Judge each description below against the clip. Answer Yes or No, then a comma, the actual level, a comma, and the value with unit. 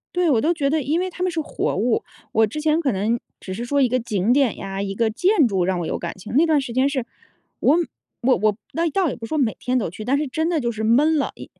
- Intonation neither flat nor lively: No, wide, 5.9 semitones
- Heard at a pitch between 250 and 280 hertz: Yes, very high, 255 Hz